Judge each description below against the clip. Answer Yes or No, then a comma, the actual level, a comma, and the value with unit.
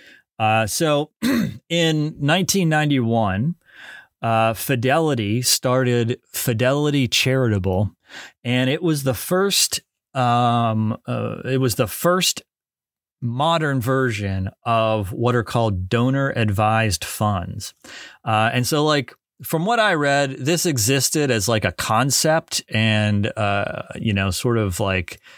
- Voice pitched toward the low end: Yes, low, 125 Hz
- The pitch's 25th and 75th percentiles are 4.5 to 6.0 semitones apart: Yes, average, 5.3 semitones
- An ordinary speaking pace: No, slow, 120 wpm